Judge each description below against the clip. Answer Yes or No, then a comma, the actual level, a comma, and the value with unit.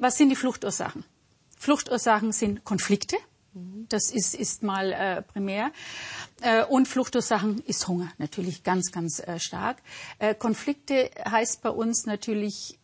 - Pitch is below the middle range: No, high, 220 Hz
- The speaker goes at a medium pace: Yes, average, 135 wpm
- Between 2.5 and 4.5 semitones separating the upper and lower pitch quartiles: Yes, average, 3.9 semitones